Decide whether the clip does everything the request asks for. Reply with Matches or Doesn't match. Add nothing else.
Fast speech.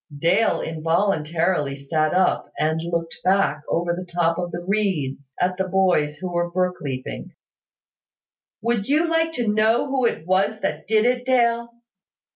Doesn't match